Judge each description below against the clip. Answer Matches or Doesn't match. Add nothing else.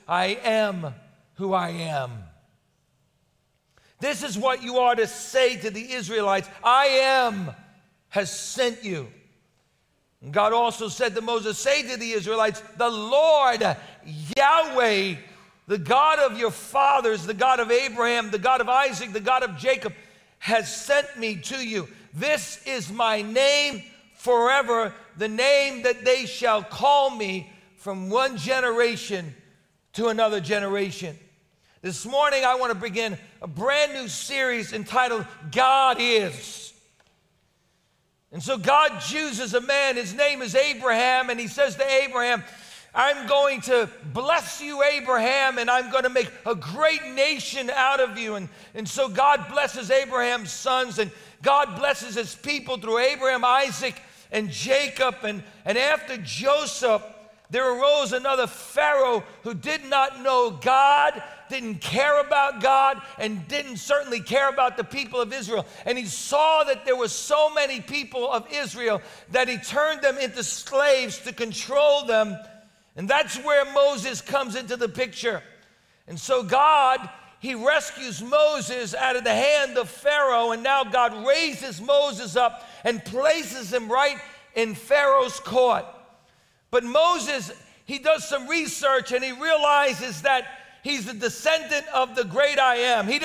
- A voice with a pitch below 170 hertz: Doesn't match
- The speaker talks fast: Doesn't match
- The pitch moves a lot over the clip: Doesn't match